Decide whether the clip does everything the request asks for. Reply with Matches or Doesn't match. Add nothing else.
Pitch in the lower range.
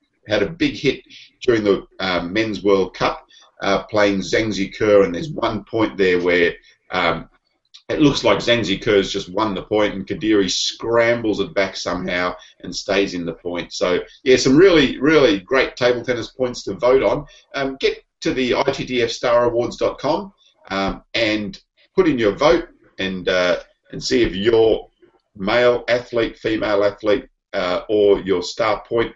Matches